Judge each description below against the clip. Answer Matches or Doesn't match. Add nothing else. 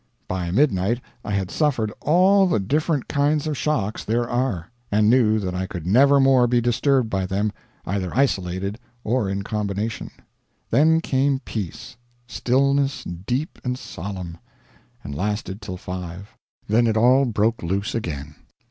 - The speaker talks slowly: Doesn't match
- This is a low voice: Matches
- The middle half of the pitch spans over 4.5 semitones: Matches